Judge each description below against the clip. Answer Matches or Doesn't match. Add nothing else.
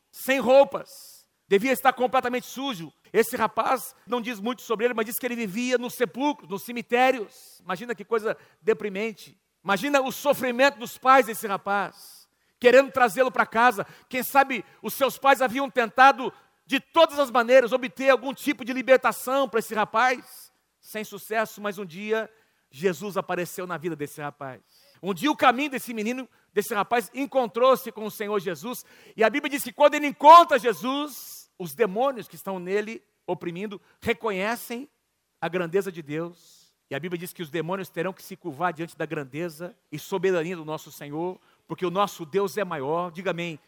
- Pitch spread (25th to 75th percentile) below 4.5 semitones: Doesn't match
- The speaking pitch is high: Matches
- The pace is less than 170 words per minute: Doesn't match